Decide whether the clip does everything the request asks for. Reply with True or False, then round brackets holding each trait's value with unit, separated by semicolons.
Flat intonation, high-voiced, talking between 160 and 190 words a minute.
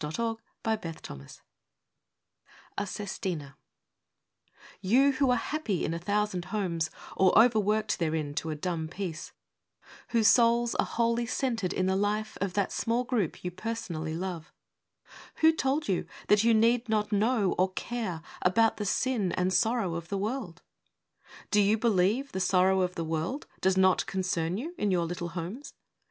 False (4.4 semitones; 200 Hz; 165 wpm)